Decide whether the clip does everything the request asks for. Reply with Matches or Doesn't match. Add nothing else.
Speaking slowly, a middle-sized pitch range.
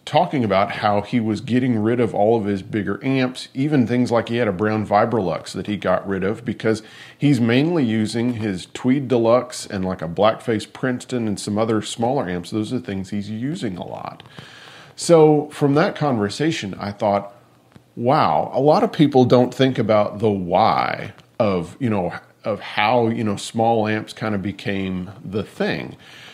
Doesn't match